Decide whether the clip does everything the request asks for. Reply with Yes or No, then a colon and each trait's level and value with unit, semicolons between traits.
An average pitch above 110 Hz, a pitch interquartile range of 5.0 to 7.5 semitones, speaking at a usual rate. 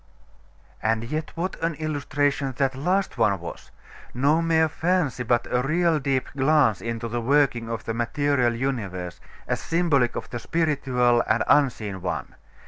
No: low, 135 Hz; average, 4.6 semitones; average, 155 wpm